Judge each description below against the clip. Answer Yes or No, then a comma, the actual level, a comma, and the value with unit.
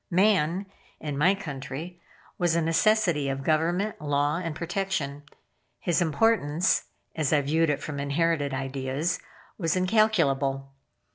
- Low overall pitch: No, medium, 160 Hz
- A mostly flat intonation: No, average, 4.1 semitones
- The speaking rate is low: Yes, slow, 125 wpm